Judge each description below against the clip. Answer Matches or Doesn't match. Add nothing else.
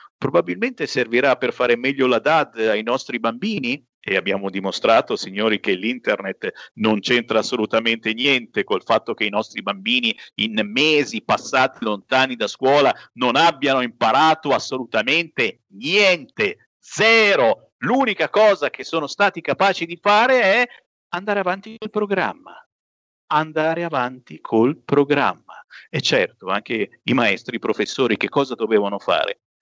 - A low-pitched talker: Doesn't match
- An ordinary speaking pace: Matches